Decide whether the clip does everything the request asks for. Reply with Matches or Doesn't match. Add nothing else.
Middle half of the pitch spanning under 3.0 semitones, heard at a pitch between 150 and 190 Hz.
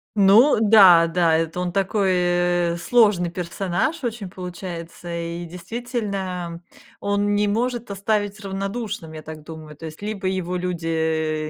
Doesn't match